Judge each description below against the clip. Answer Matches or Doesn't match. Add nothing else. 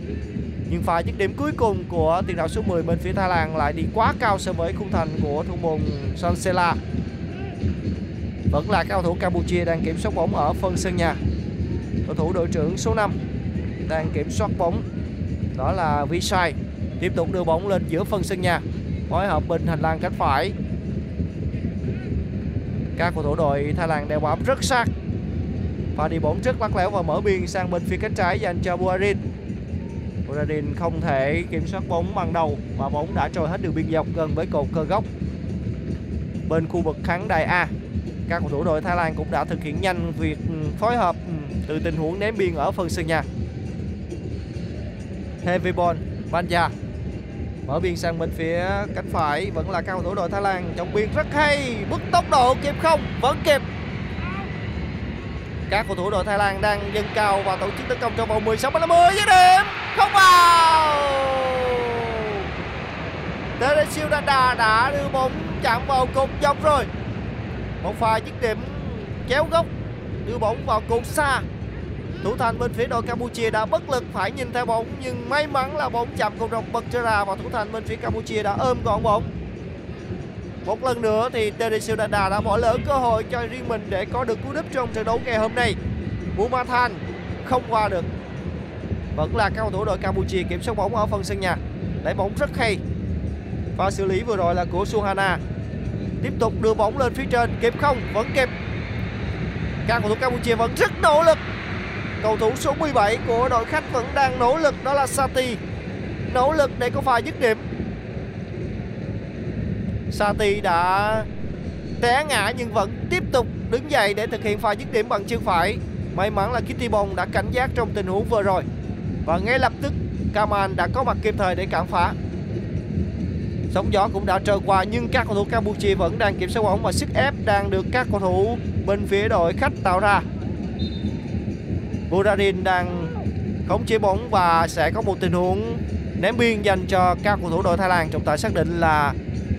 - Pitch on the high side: Matches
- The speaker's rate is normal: Matches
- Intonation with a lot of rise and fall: Matches